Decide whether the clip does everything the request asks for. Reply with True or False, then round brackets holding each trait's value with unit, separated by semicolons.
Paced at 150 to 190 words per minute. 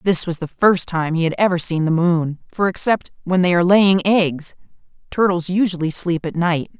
False (205 wpm)